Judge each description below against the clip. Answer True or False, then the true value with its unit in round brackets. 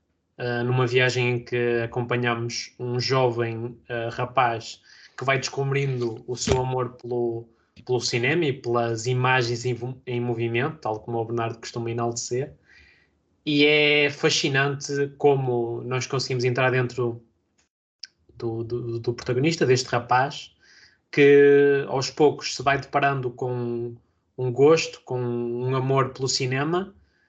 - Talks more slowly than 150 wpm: True (130 wpm)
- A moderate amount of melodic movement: False (2.2 semitones)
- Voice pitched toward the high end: False (125 Hz)